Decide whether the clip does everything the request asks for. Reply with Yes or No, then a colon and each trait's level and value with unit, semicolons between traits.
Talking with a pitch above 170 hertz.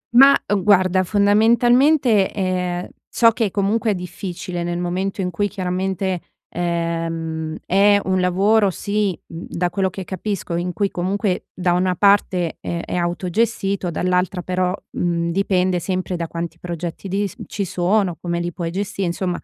Yes: medium, 185 Hz